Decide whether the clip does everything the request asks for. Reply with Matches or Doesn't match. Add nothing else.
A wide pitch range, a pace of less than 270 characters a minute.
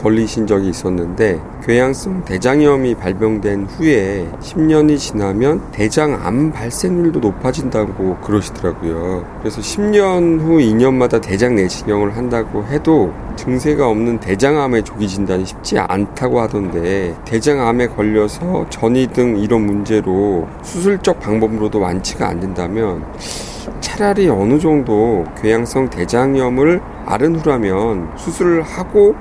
Doesn't match